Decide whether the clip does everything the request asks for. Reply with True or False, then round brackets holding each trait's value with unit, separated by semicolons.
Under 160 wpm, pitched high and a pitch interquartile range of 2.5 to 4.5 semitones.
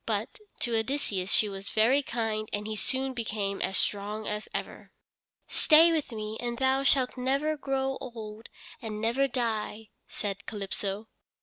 True (150 wpm; 225 Hz; 3.9 semitones)